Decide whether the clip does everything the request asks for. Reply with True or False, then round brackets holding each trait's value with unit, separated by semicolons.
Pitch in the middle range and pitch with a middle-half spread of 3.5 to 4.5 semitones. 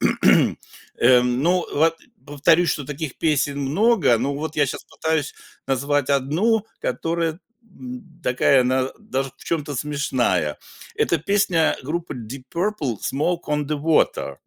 True (150 Hz; 4.0 semitones)